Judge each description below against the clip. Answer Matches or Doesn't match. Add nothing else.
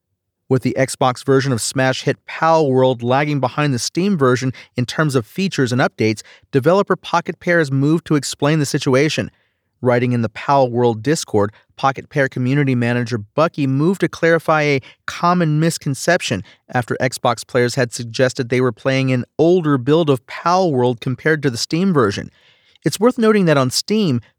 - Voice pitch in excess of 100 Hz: Matches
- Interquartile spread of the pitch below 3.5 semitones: Doesn't match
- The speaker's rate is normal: Matches